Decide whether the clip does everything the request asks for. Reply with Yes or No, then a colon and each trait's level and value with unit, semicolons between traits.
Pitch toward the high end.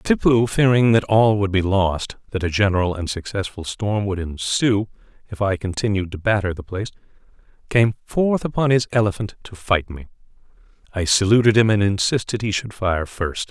No: low, 100 Hz